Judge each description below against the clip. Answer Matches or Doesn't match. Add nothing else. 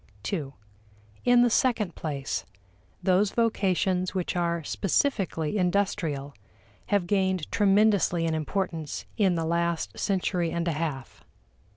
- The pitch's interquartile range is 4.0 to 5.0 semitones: Doesn't match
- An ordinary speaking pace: Doesn't match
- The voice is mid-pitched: Matches